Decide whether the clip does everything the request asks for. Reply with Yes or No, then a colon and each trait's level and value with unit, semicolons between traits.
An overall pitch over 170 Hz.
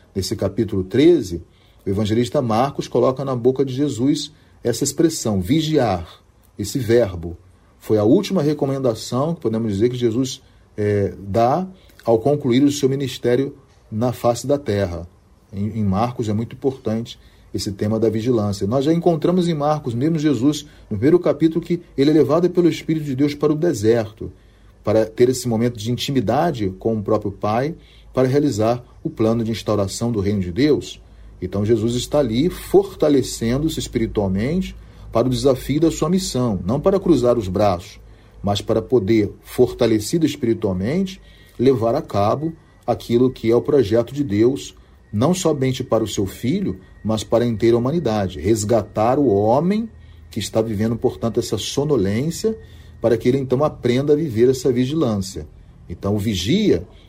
No: low, 115 Hz